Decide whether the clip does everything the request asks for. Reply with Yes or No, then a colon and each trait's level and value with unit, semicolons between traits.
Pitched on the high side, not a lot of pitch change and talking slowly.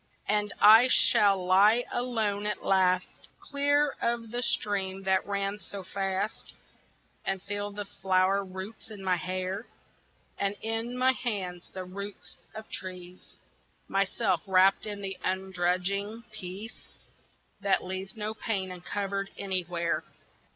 Yes: high, 195 Hz; narrow, 2.1 semitones; slow, 125 wpm